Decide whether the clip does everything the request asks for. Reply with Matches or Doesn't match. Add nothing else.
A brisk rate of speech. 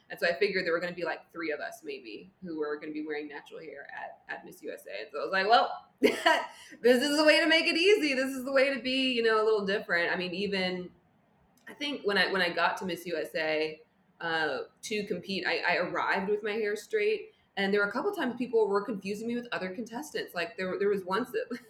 Matches